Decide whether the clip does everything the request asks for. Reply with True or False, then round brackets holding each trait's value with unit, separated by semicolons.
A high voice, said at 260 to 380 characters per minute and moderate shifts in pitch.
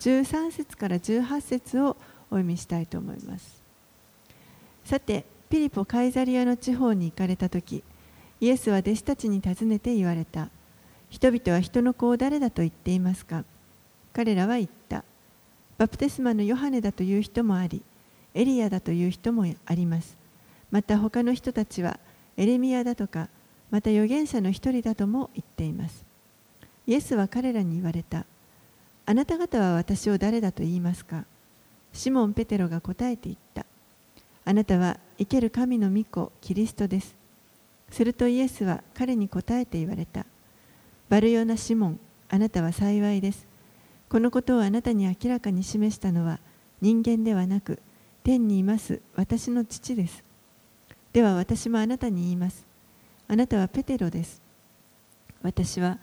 True (210 Hz; 300 characters per minute; 5.0 semitones)